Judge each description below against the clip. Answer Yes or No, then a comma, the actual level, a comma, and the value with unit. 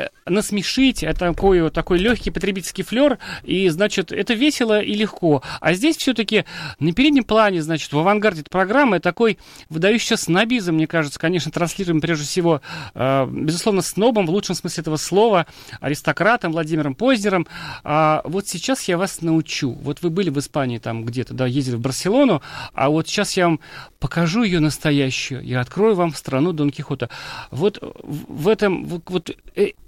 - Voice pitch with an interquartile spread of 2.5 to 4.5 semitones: No, average, 5.2 semitones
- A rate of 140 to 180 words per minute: Yes, fast, 160 wpm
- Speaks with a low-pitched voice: No, medium, 175 Hz